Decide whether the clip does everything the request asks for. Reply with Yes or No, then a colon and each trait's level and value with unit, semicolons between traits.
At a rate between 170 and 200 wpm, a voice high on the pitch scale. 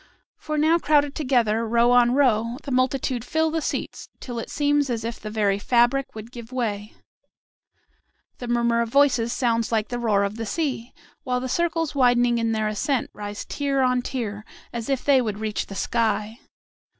Yes: average, 185 wpm; high, 240 Hz